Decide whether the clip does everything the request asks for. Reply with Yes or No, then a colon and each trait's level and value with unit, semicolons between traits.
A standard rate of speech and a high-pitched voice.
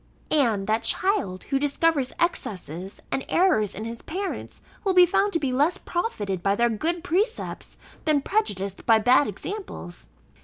Yes: average, 155 wpm; very high, 275 Hz